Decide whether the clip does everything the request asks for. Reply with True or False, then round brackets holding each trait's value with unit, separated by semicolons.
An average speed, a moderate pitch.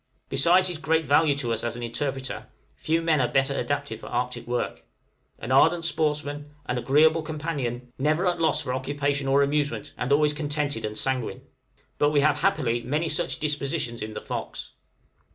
True (175 wpm; 145 Hz)